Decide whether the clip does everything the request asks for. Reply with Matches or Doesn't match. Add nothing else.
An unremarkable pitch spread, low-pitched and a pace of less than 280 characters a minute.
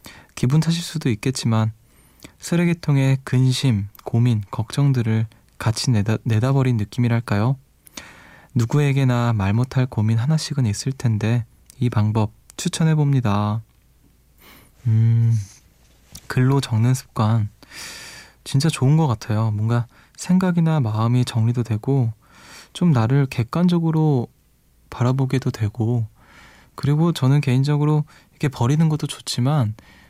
Matches